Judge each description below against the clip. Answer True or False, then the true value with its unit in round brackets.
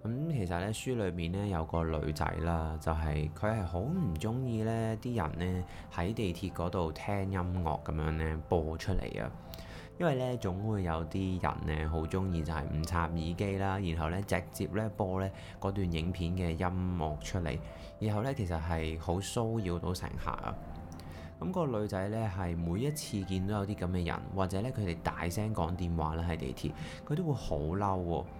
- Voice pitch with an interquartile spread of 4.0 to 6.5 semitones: False (3.4 semitones)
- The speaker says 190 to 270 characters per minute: True (265 characters per minute)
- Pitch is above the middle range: False (90 Hz)